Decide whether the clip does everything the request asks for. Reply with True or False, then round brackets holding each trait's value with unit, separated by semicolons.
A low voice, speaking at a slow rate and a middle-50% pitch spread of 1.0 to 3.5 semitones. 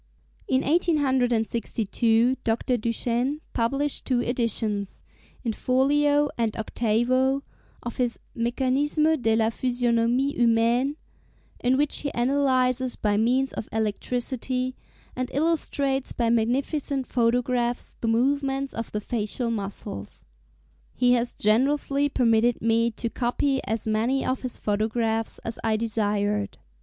False (245 Hz; 115 wpm; 2.8 semitones)